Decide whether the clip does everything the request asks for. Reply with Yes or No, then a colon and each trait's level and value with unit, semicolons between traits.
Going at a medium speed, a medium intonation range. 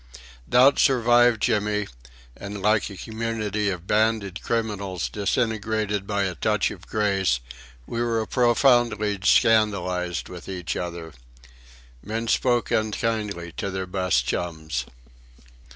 No: slow, 115 wpm; average, 3.4 semitones